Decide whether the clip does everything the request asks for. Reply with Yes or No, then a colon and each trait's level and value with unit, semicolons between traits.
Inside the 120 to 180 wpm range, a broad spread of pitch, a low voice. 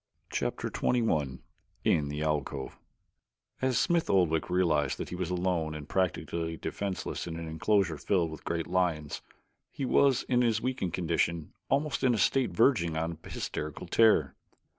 Yes: average, 150 wpm; wide, 5.9 semitones; very low, 85 Hz